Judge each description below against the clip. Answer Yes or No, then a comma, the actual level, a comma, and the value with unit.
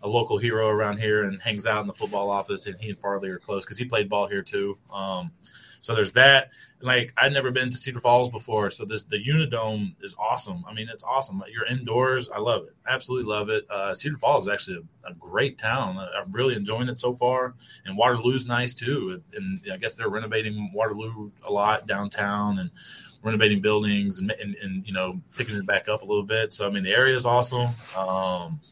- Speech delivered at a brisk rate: Yes, fast, 225 wpm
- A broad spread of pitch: No, average, 3.9 semitones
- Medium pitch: No, low, 110 Hz